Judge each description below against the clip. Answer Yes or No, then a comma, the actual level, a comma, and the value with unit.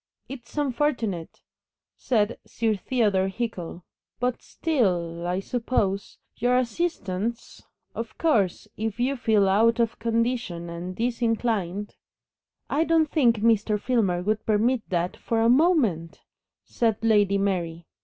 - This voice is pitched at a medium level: No, high, 225 Hz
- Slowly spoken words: Yes, slow, 125 wpm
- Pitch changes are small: No, average, 4.2 semitones